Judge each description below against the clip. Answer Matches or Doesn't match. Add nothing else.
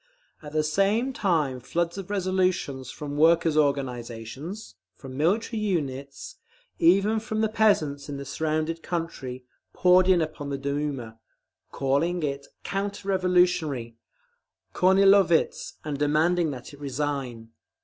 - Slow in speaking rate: Matches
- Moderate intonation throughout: Matches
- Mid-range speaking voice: Matches